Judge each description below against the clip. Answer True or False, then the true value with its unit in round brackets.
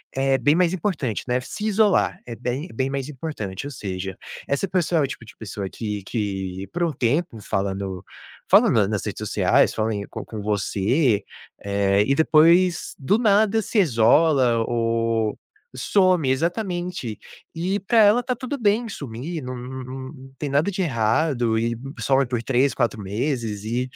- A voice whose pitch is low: True (130 Hz)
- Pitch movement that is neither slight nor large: False (7.4 semitones)